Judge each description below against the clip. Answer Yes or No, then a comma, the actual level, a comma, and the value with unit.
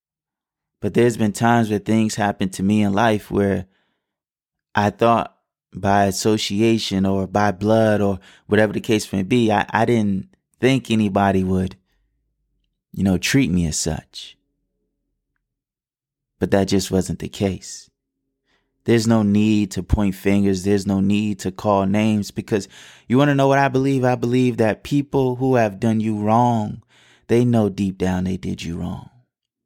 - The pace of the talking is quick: No, average, 160 wpm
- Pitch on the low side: Yes, low, 105 Hz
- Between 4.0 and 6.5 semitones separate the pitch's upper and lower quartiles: No, average, 3.0 semitones